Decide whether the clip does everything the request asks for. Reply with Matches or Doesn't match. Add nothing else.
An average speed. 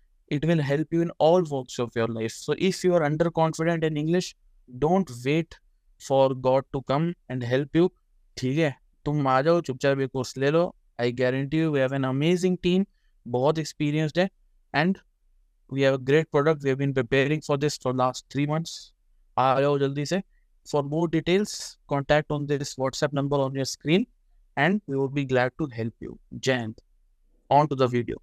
Doesn't match